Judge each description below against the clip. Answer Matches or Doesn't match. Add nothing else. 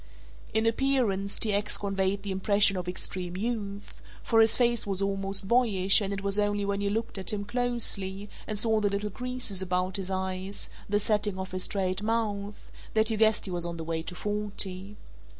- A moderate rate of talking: Matches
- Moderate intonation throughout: Doesn't match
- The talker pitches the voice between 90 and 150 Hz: Doesn't match